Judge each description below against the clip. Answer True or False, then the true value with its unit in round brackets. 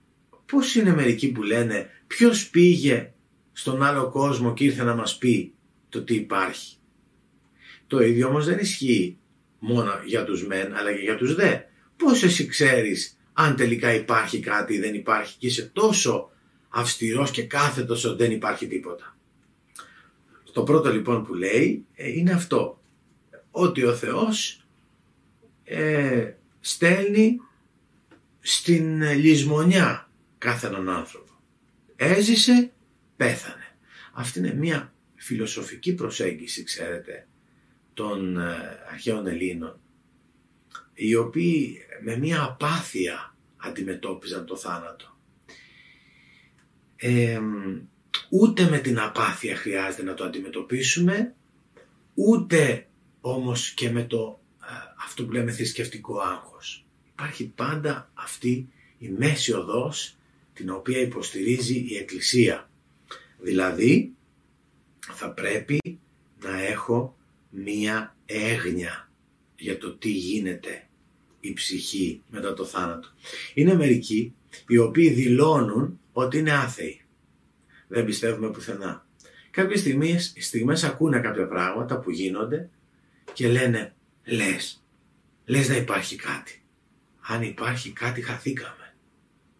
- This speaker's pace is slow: True (110 wpm)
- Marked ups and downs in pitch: True (6.5 semitones)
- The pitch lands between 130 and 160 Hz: False (120 Hz)